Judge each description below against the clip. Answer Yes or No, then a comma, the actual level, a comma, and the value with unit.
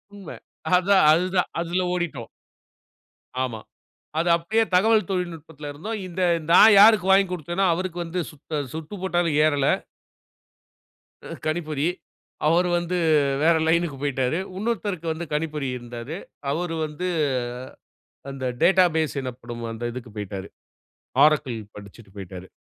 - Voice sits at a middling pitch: Yes, medium, 165 Hz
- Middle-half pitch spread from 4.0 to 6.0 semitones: Yes, average, 4.7 semitones